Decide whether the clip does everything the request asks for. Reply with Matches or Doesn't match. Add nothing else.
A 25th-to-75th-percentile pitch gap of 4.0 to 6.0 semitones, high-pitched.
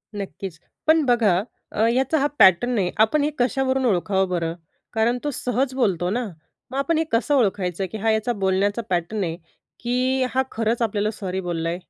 Matches